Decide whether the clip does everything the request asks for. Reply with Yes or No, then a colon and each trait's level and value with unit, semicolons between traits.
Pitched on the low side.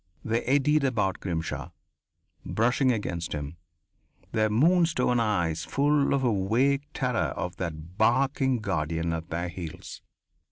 Yes: low, 110 Hz